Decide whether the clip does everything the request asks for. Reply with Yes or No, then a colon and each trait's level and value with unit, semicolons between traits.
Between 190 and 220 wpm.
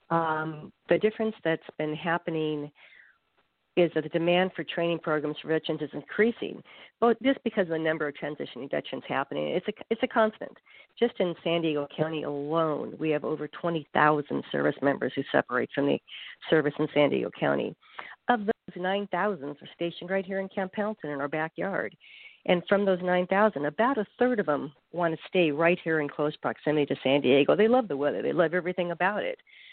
Yes: average, 200 wpm